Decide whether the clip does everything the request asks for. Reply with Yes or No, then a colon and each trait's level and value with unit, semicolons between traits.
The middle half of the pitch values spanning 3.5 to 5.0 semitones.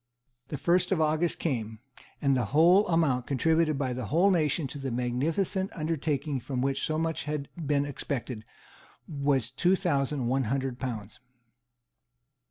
Yes: average, 4.0 semitones